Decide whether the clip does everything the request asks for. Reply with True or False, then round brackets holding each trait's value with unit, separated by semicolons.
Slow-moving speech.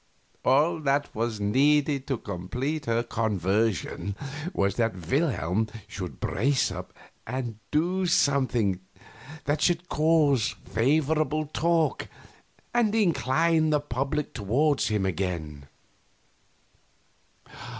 True (100 wpm)